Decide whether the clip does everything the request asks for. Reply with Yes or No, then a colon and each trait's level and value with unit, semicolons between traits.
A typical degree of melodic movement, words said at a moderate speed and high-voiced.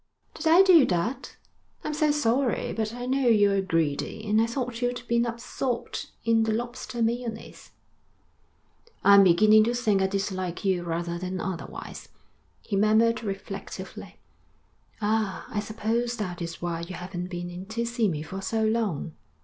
Yes: average, 4.0 semitones; average, 155 wpm; high, 215 Hz